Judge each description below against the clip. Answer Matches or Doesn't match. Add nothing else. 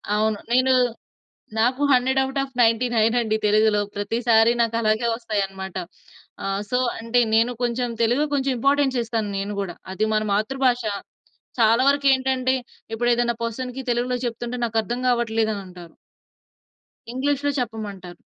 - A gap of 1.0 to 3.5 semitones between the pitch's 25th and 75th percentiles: Matches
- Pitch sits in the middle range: Doesn't match